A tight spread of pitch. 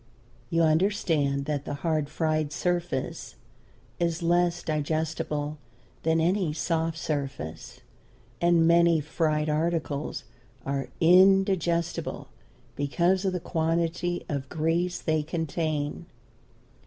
Yes: narrow, 2.2 semitones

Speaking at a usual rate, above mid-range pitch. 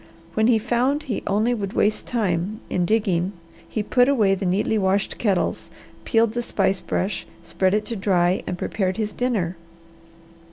Yes: average, 165 wpm; high, 205 Hz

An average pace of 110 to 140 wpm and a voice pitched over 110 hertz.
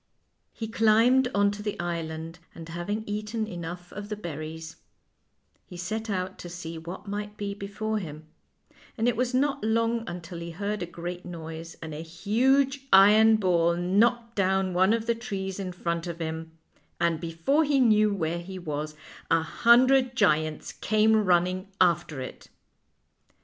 No: average, 165 wpm; high, 190 Hz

